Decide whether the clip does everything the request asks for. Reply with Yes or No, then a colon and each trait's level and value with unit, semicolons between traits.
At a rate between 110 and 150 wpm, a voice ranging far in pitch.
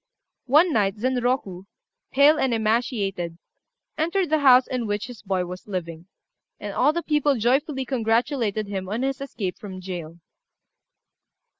Yes: average, 140 wpm; wide, 5.7 semitones